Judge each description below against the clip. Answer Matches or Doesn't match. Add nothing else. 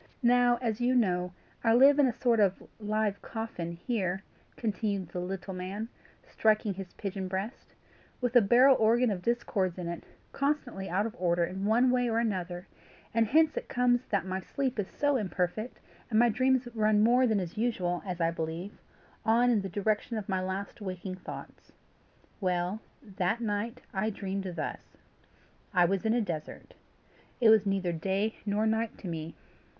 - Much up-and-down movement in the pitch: Doesn't match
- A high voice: Matches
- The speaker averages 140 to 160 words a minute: Doesn't match